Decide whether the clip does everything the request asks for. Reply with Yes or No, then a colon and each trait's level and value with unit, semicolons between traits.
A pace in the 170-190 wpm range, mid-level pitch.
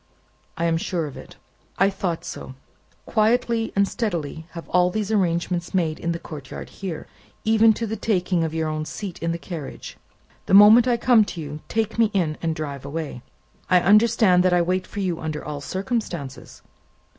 Yes: average, 185 wpm; medium, 180 Hz